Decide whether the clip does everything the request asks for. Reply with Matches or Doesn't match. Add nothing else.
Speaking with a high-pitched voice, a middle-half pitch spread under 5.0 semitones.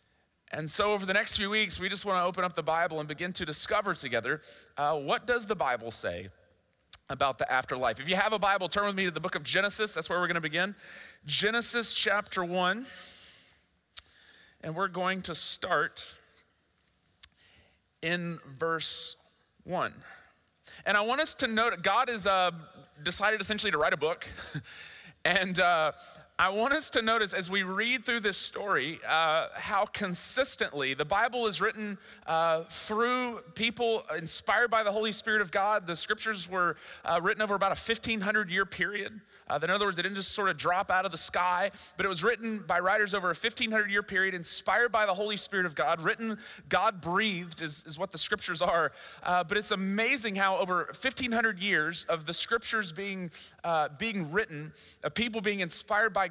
Matches